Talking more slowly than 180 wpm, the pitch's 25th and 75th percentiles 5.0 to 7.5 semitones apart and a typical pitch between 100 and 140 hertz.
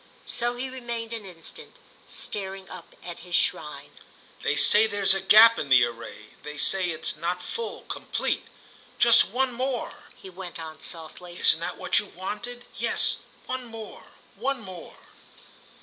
No: average, 150 wpm; wide, 5.5 semitones; high, 200 Hz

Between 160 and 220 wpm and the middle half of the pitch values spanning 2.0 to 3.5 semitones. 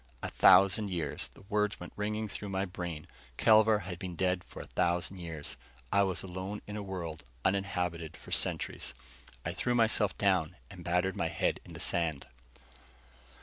Yes: average, 170 wpm; average, 2.8 semitones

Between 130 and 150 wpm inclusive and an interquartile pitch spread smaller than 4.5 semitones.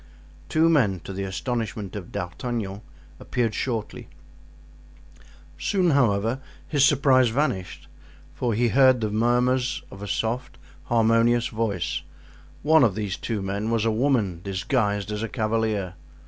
Yes: slow, 135 wpm; average, 3.8 semitones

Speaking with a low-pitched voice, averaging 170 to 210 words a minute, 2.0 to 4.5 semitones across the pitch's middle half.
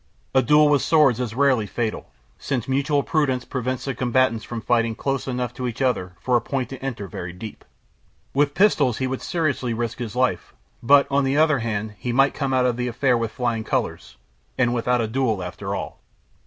Yes: low, 125 Hz; fast, 205 wpm; average, 2.9 semitones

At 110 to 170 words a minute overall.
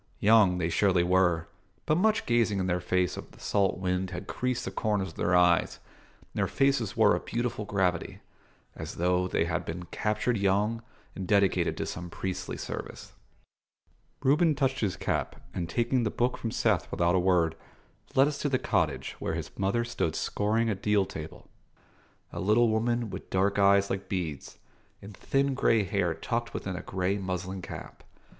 No: average, 180 wpm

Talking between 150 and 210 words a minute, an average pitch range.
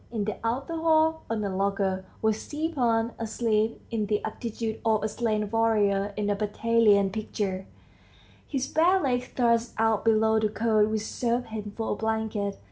No: average, 165 wpm; narrow, 1.9 semitones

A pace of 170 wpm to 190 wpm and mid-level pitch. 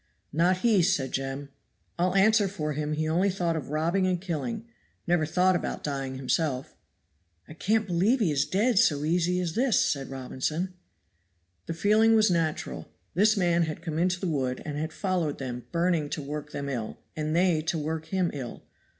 Yes: average, 185 wpm; medium, 165 Hz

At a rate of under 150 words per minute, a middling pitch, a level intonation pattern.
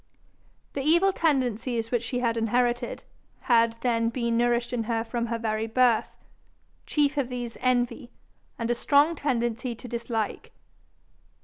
No: average, 140 wpm; high, 240 Hz; narrow, 1.6 semitones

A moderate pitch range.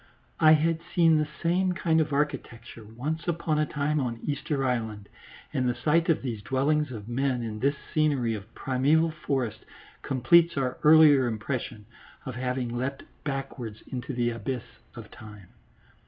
Yes: average, 4.3 semitones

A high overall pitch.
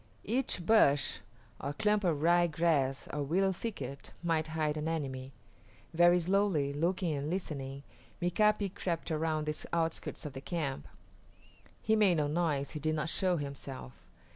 No: medium, 160 Hz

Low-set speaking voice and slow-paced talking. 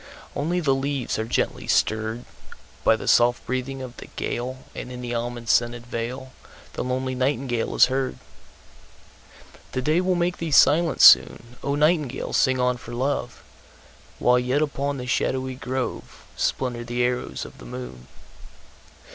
Yes: low, 125 Hz; slow, 130 wpm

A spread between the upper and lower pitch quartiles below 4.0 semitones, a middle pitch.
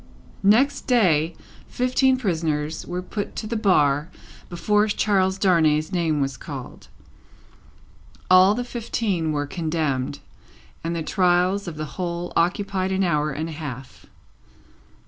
No: average, 4.5 semitones; medium, 175 Hz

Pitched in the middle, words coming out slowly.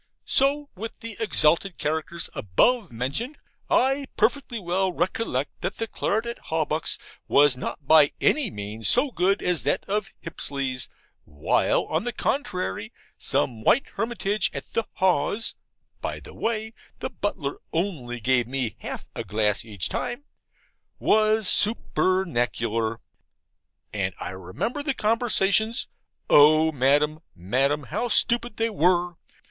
Yes: medium, 175 Hz; slow, 130 wpm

